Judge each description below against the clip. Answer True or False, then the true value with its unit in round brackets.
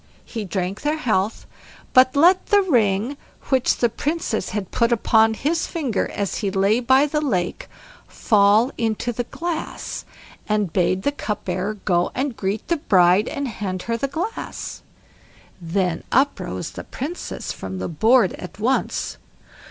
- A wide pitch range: True (6.1 semitones)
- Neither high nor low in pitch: False (225 Hz)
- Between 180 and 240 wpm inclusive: False (150 wpm)